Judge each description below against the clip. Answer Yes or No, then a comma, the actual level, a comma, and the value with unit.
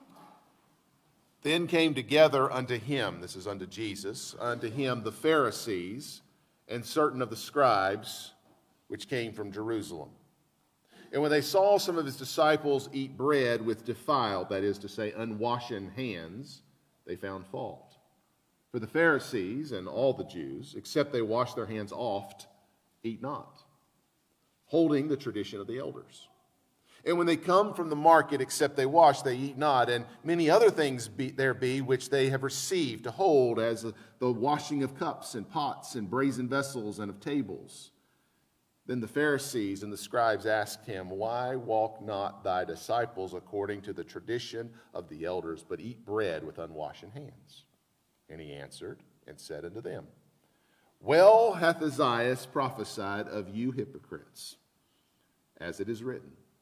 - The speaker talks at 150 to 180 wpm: Yes, average, 155 wpm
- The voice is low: Yes, low, 125 Hz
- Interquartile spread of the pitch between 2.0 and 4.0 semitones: No, average, 4.8 semitones